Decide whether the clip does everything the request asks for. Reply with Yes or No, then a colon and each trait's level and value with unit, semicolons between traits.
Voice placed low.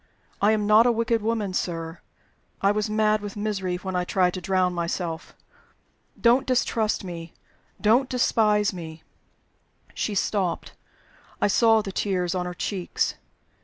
No: high, 200 Hz